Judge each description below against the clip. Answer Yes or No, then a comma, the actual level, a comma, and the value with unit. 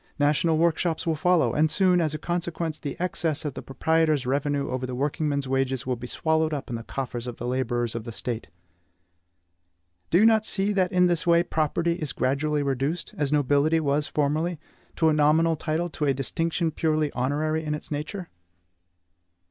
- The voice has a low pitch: No, medium, 155 Hz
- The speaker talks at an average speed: Yes, average, 185 wpm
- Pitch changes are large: No, average, 3.2 semitones